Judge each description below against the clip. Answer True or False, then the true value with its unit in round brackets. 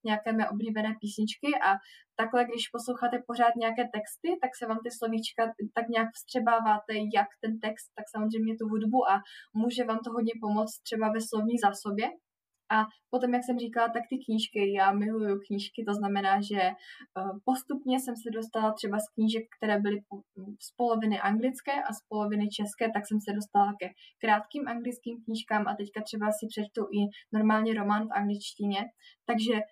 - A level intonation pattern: True (2.0 semitones)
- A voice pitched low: False (220 Hz)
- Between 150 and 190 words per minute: True (170 wpm)